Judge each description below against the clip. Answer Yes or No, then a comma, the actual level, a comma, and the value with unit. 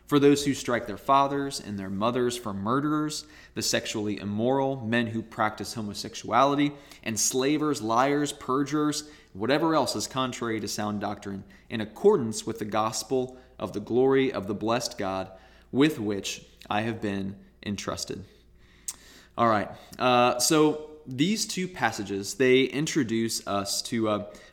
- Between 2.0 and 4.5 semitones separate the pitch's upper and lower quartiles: No, average, 5.0 semitones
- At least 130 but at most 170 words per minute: Yes, average, 140 wpm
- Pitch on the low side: Yes, low, 115 Hz